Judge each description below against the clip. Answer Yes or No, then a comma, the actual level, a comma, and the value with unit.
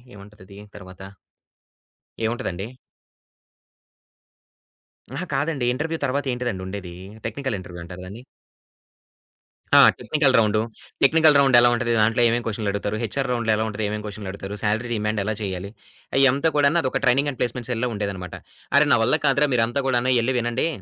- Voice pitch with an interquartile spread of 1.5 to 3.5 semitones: No, average, 4.6 semitones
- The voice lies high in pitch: No, low, 115 Hz